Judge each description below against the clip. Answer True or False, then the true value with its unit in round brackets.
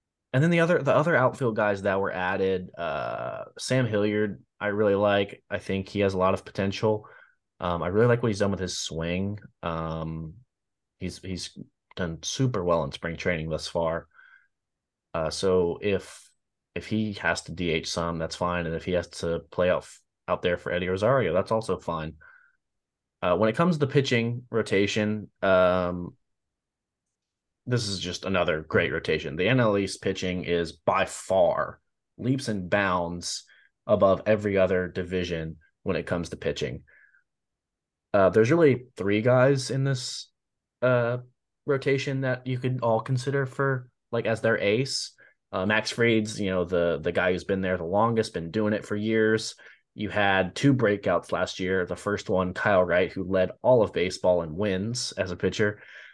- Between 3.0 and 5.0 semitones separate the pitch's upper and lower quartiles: True (4.1 semitones)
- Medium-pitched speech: False (100 Hz)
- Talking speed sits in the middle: True (175 wpm)